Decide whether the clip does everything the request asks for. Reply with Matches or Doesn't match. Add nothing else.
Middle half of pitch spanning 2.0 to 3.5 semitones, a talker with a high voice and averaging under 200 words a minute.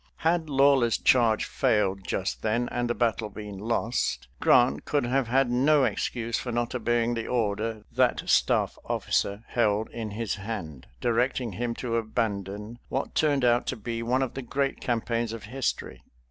Doesn't match